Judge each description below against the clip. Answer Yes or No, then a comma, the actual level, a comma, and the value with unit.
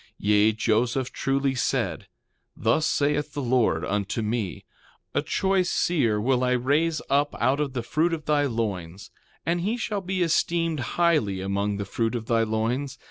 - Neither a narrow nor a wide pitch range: No, wide, 5.7 semitones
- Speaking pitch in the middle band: No, low, 130 Hz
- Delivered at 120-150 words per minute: No, average, 170 wpm